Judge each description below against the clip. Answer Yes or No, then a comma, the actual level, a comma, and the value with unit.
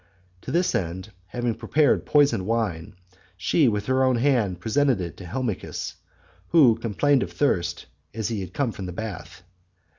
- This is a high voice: No, low, 115 Hz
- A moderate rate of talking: Yes, average, 155 wpm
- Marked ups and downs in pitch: Yes, wide, 5.9 semitones